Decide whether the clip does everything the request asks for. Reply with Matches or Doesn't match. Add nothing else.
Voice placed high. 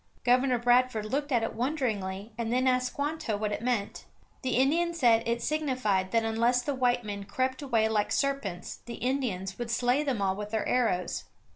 Matches